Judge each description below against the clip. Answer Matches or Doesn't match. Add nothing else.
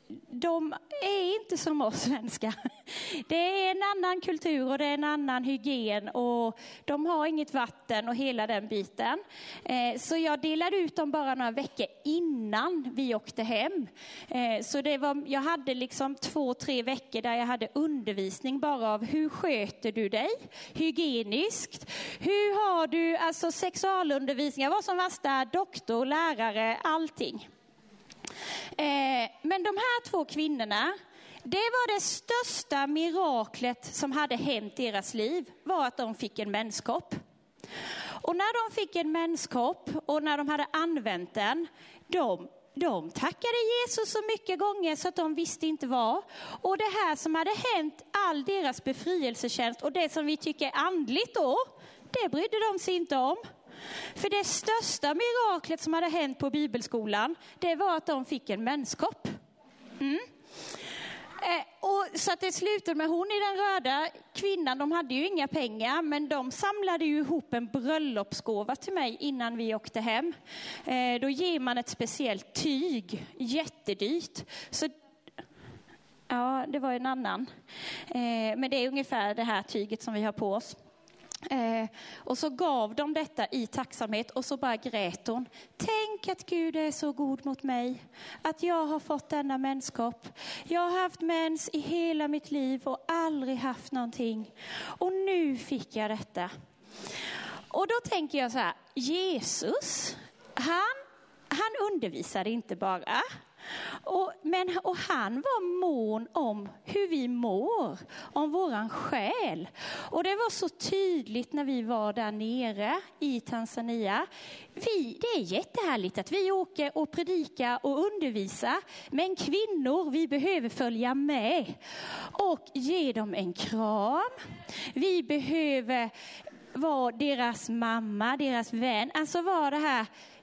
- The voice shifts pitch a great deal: Matches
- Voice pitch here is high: Matches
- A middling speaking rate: Matches